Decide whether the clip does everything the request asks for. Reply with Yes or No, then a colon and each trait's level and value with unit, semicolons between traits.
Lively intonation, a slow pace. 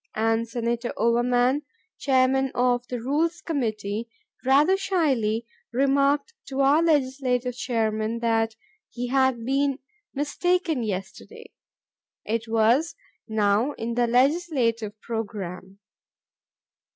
No: average, 3.6 semitones; slow, 100 wpm